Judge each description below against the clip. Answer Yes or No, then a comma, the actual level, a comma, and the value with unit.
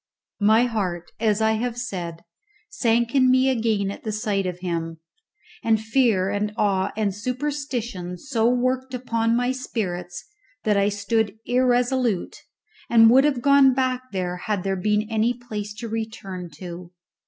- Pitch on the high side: Yes, high, 220 Hz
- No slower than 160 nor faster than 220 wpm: No, average, 150 wpm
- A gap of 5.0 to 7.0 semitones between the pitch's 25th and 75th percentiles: No, average, 4.1 semitones